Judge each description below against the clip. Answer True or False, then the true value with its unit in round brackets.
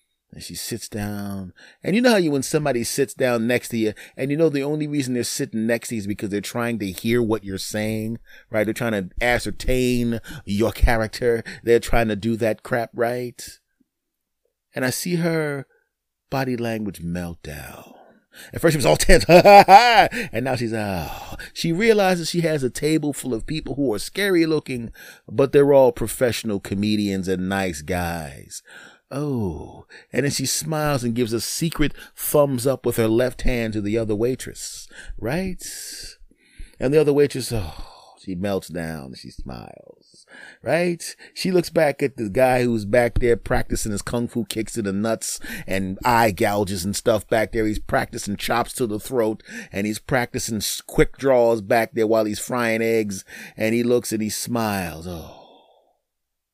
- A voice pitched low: True (115 Hz)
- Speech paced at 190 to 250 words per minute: False (180 wpm)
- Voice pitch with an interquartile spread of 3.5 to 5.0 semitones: True (4.6 semitones)